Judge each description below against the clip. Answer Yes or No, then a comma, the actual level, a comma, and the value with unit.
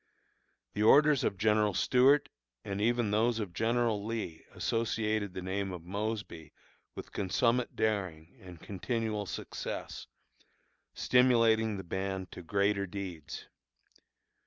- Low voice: Yes, low, 105 Hz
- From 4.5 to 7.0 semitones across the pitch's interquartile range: No, average, 3.2 semitones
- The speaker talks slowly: Yes, slow, 115 wpm